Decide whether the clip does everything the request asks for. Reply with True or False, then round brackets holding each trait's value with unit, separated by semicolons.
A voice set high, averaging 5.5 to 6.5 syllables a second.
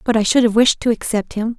True (225 Hz; 6.0 syllables/s)